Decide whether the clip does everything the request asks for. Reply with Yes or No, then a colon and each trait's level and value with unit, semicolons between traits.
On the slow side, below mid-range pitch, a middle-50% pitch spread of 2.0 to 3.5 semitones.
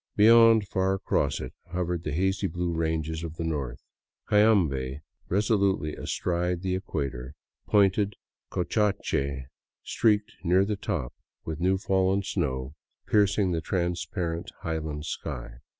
No: slow, 125 wpm; very low, 90 Hz; average, 4.2 semitones